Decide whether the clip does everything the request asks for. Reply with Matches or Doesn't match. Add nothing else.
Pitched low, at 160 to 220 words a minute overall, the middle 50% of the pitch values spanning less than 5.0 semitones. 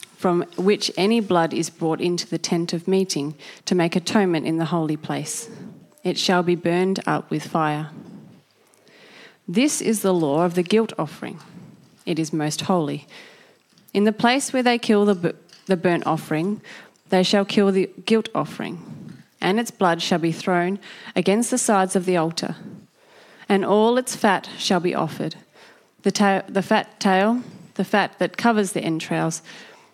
Doesn't match